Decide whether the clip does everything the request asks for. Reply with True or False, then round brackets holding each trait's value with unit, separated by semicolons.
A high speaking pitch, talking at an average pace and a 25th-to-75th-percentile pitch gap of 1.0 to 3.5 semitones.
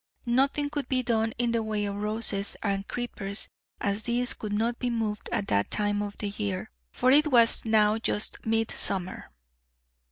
True (220 Hz; 165 wpm; 2.8 semitones)